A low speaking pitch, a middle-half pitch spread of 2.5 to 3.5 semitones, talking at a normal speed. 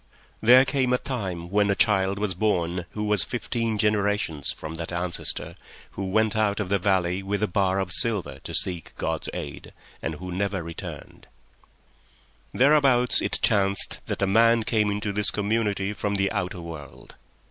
Yes: low, 100 Hz; average, 3.0 semitones; average, 170 wpm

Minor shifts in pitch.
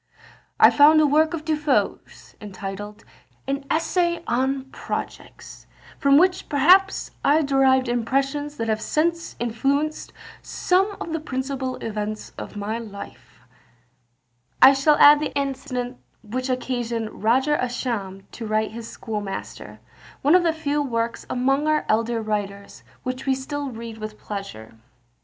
No: average, 4.9 semitones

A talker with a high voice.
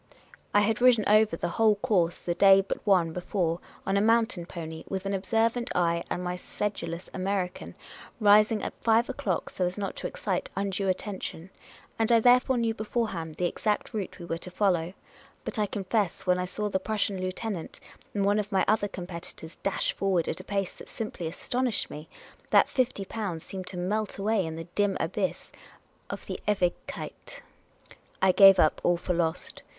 Yes: high, 195 Hz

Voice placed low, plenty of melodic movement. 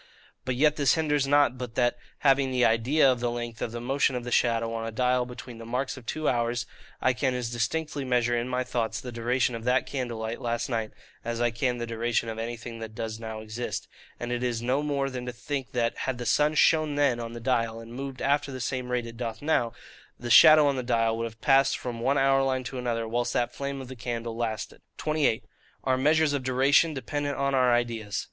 No: low, 125 Hz; narrow, 2.6 semitones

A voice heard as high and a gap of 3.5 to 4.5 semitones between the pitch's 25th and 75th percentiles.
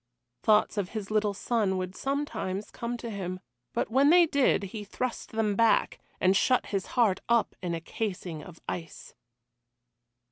Yes: high, 210 Hz; average, 3.9 semitones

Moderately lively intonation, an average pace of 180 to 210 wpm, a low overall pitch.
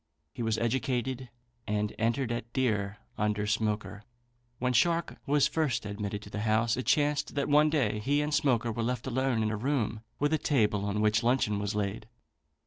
Yes: average, 4.0 semitones; average, 185 wpm; low, 115 Hz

